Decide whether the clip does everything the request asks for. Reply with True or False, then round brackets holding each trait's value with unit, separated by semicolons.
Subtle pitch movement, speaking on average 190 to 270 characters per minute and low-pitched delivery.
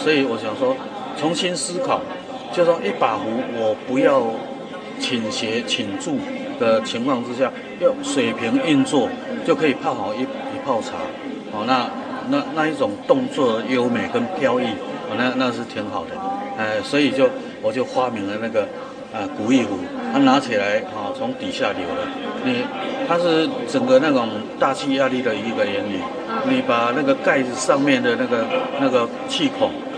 False (0.5 semitones; 240 characters per minute; 265 Hz)